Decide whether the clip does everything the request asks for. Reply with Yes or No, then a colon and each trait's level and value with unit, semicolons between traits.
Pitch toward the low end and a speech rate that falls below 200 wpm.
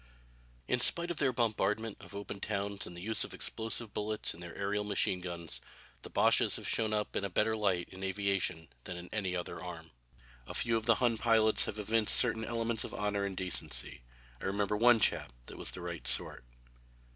No: low, 105 Hz; fast, 205 wpm